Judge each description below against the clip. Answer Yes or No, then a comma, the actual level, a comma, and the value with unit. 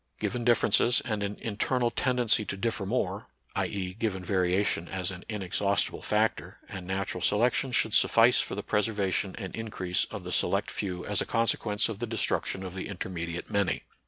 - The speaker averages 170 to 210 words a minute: Yes, average, 175 wpm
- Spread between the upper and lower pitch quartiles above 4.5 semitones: No, average, 3.3 semitones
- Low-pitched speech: Yes, low, 100 Hz